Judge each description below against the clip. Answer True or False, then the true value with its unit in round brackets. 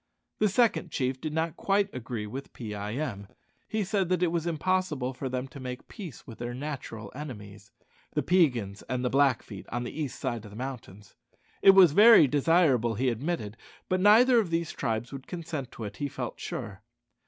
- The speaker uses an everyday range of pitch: False (6.4 semitones)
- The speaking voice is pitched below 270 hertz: True (135 Hz)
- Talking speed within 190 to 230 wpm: True (195 wpm)